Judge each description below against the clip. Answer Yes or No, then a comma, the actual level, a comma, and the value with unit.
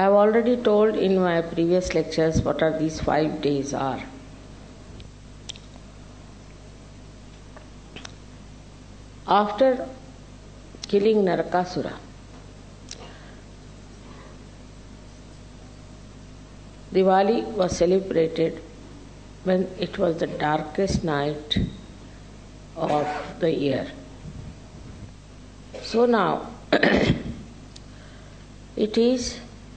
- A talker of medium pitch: No, low, 130 Hz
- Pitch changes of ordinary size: No, wide, 6.9 semitones